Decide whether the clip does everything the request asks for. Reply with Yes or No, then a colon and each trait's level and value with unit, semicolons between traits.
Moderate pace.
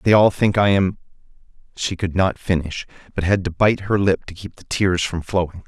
No: fast, 220 wpm